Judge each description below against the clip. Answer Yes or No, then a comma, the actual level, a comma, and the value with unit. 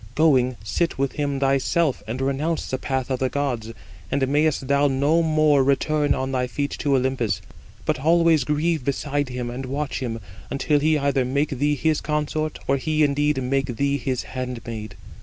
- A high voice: No, medium, 140 Hz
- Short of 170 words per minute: No, average, 175 wpm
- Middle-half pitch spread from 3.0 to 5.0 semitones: No, narrow, 2.5 semitones